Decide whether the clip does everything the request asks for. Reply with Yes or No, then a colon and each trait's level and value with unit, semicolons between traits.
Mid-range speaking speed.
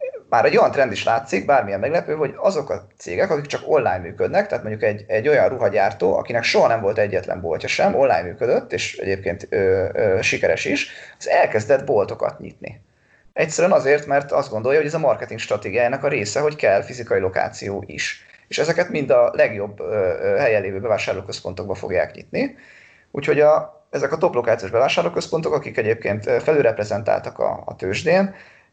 No: fast, 170 wpm